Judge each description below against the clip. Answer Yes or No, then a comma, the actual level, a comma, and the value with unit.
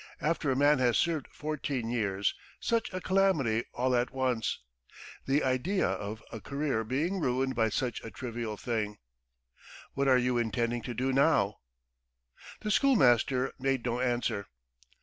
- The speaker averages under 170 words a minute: Yes, average, 150 wpm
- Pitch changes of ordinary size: Yes, average, 3.6 semitones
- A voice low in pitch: Yes, low, 130 Hz